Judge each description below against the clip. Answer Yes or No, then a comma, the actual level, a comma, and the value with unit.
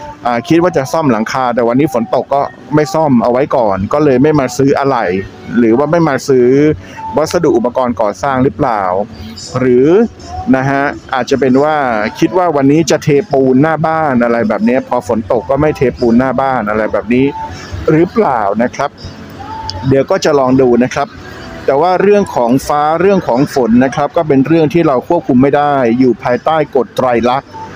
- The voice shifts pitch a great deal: No, average, 4.2 semitones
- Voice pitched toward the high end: No, medium, 140 Hz